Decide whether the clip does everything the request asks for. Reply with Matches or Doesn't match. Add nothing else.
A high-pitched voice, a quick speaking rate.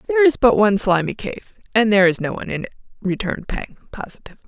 Matches